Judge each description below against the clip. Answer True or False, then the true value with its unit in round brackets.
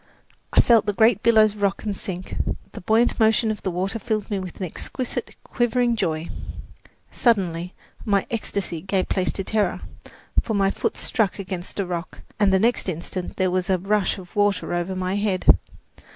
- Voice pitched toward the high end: True (195 Hz)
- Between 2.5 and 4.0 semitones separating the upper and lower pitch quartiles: True (2.9 semitones)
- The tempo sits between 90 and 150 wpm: False (180 wpm)